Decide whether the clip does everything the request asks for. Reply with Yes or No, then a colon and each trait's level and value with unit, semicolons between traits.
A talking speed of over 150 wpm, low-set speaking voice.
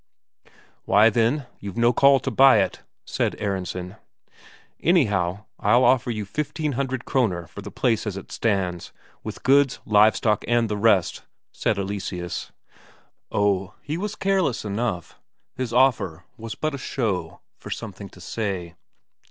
No: average, 145 wpm; low, 110 Hz